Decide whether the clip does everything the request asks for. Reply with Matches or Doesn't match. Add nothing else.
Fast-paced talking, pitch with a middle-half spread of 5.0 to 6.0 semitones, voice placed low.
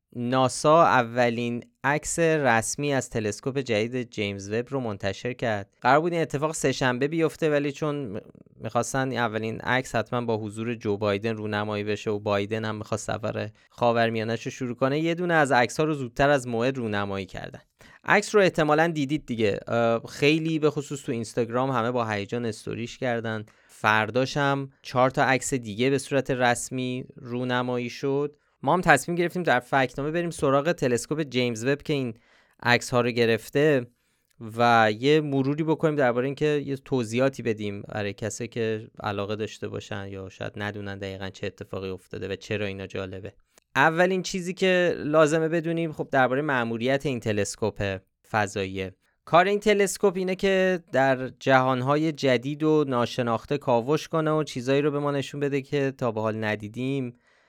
Doesn't match